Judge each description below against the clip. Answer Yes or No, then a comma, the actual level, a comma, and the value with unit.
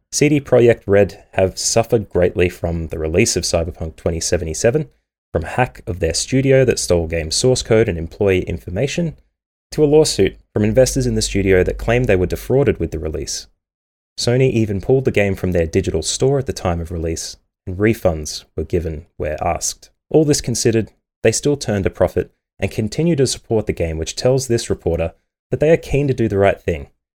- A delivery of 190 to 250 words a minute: Yes, average, 195 wpm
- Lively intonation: Yes, wide, 6.4 semitones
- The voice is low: Yes, low, 100 Hz